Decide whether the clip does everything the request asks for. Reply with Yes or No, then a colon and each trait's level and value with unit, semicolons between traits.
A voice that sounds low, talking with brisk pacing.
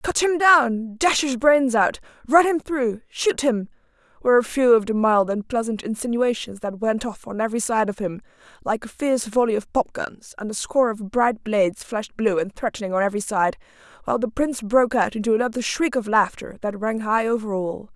No: high, 230 Hz; fast, 215 wpm